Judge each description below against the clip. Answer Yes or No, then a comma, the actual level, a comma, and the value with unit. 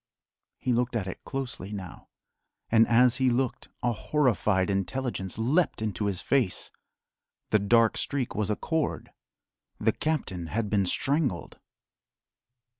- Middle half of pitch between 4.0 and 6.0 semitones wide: Yes, average, 4.7 semitones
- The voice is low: Yes, low, 115 Hz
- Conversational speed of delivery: No, slow, 130 wpm